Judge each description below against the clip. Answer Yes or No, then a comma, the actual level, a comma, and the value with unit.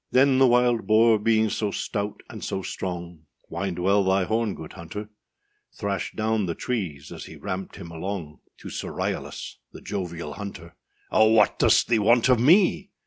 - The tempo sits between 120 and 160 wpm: No, average, 175 wpm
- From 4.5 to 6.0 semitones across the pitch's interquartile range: No, average, 4.1 semitones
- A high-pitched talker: No, low, 100 Hz